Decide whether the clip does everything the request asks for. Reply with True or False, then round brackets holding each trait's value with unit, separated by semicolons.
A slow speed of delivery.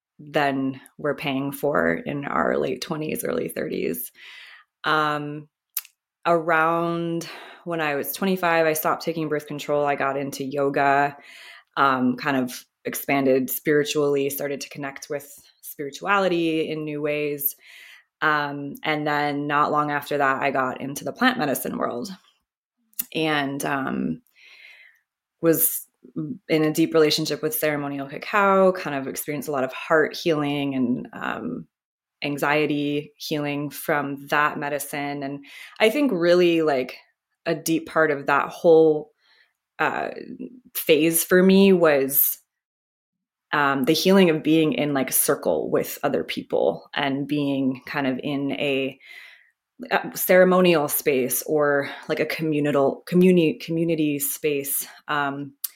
True (130 wpm)